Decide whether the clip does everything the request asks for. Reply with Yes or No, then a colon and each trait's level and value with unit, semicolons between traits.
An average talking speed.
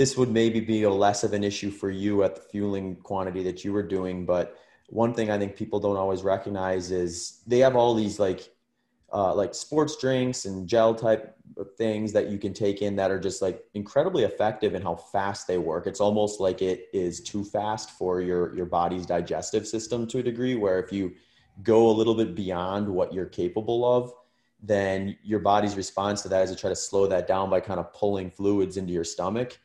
No: fast, 215 wpm